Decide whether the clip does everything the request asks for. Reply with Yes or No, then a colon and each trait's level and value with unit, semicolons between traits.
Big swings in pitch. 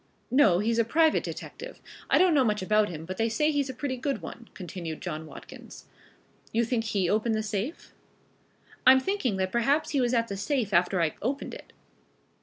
Yes: wide, 5.8 semitones